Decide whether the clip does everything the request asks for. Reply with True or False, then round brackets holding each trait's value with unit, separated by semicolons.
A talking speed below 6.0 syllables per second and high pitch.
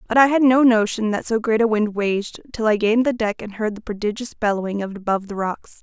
False (6.1 syllables/s; 215 Hz)